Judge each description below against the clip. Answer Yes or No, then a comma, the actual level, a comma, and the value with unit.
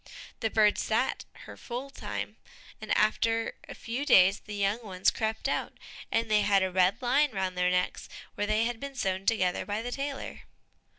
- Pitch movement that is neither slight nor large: Yes, average, 3.7 semitones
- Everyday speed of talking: Yes, average, 185 wpm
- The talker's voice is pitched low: No, high, 215 Hz